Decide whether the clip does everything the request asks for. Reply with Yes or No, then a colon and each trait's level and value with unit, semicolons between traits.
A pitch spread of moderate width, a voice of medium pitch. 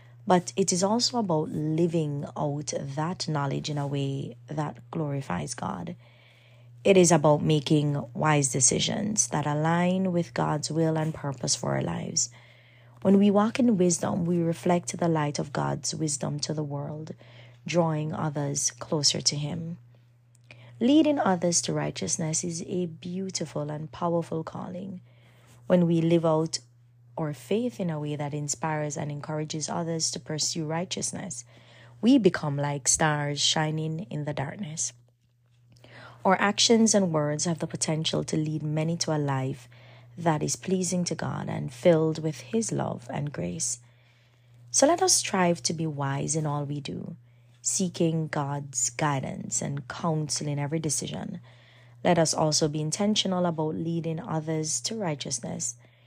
Yes: average, 3.9 semitones; medium, 155 Hz